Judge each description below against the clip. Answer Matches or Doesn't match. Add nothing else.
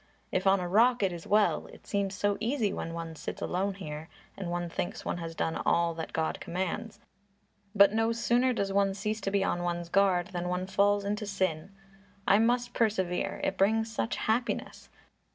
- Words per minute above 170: Matches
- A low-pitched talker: Doesn't match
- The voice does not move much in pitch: Doesn't match